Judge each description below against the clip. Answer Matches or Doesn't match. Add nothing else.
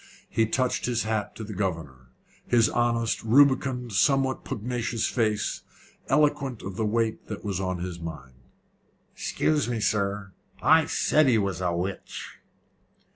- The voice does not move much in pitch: Doesn't match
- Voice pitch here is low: Matches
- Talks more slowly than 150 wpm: Matches